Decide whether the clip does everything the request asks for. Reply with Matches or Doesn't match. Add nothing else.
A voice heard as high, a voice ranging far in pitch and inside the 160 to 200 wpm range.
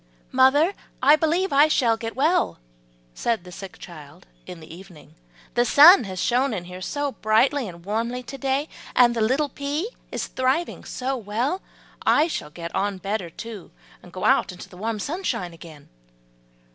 Matches